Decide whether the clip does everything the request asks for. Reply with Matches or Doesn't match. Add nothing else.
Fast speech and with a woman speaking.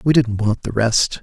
Doesn't match